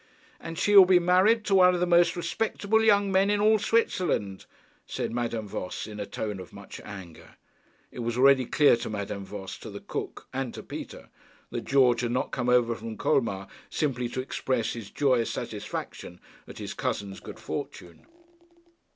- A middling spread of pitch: No, wide, 8.9 semitones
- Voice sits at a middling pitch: No, low, 125 Hz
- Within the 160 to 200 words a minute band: Yes, average, 185 wpm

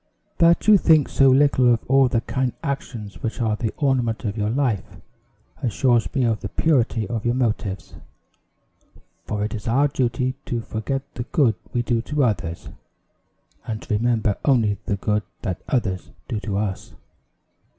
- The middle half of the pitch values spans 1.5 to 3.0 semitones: No, average, 3.7 semitones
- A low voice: Yes, low, 120 Hz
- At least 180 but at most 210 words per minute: No, average, 165 wpm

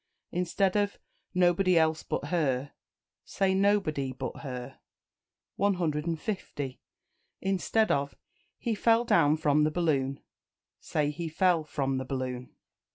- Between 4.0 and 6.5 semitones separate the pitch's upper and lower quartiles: Yes, average, 5.3 semitones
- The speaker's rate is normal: No, slow, 115 wpm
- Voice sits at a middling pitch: Yes, medium, 160 Hz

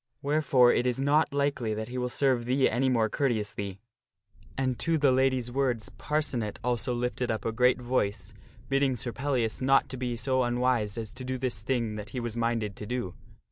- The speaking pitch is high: No, low, 125 Hz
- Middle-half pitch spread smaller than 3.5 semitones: Yes, narrow, 2.5 semitones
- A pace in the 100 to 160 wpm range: No, average, 195 wpm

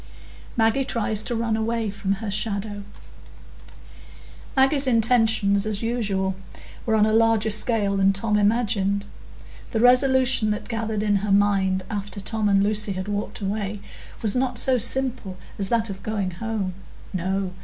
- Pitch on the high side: Yes, high, 215 Hz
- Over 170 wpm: No, average, 150 wpm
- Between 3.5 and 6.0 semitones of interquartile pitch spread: No, narrow, 2.4 semitones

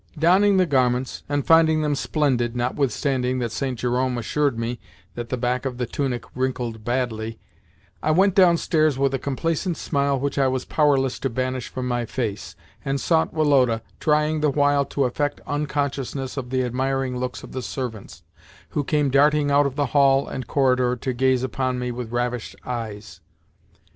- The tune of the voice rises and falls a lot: No, average, 2.7 semitones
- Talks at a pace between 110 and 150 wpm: No, average, 175 wpm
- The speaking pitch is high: No, low, 130 Hz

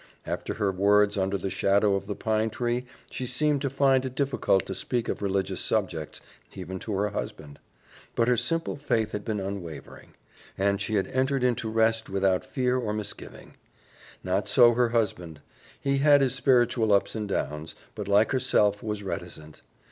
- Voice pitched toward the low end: Yes, low, 105 Hz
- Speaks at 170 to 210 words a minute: Yes, average, 175 wpm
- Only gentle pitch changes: No, average, 4.2 semitones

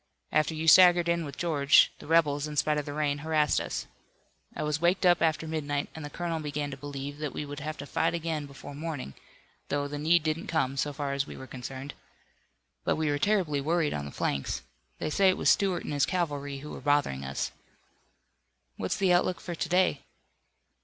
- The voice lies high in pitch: No, medium, 150 Hz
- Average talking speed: No, fast, 210 wpm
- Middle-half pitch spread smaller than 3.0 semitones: Yes, narrow, 2.6 semitones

